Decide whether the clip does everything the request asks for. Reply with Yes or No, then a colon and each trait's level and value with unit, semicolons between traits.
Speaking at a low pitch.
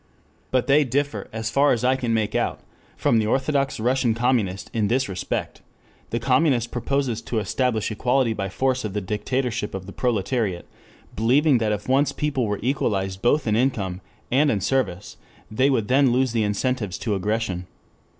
Yes: low, 120 Hz